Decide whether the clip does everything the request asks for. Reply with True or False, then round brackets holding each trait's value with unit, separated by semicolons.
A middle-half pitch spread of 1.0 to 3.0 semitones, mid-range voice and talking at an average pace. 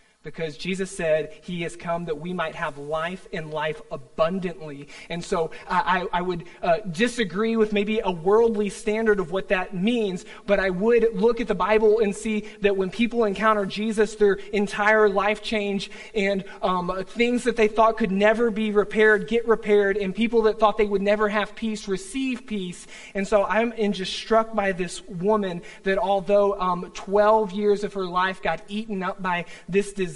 False (2.5 semitones; 205 Hz; 185 wpm)